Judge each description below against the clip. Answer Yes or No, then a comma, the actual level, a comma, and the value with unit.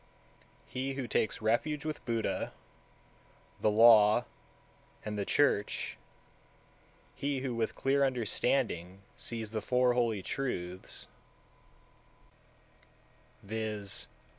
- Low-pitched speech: Yes, low, 115 Hz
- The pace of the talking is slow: Yes, slow, 100 wpm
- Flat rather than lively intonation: No, average, 3.7 semitones